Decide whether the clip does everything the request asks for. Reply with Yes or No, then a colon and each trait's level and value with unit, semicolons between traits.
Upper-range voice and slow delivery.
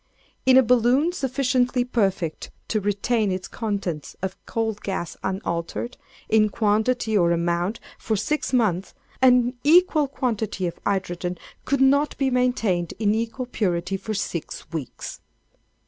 Yes: high, 220 Hz; slow, 130 wpm